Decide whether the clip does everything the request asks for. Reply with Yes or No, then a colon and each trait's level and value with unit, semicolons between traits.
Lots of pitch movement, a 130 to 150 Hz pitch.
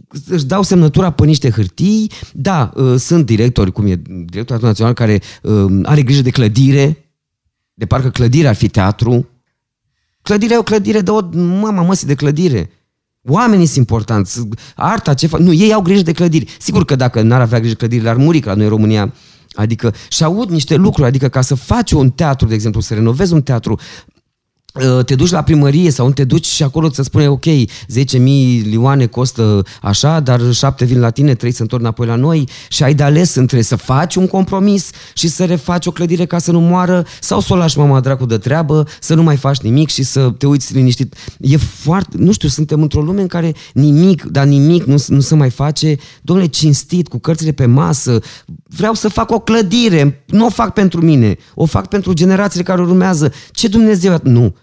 Yes: wide, 5.9 semitones; medium, 140 Hz